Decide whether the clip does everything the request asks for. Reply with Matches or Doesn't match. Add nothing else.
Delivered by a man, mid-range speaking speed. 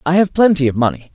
Doesn't match